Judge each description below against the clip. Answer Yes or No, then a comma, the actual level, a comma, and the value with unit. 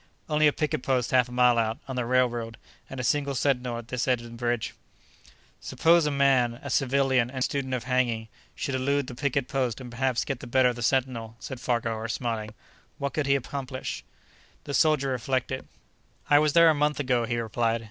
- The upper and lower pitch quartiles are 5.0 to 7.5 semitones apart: No, narrow, 2.5 semitones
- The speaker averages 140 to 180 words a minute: No, average, 200 wpm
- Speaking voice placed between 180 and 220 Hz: No, low, 130 Hz